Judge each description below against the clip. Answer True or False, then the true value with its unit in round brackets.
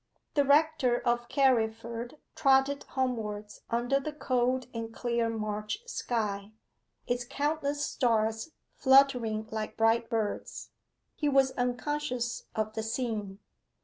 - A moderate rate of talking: False (115 wpm)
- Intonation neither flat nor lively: True (3.5 semitones)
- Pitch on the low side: False (240 Hz)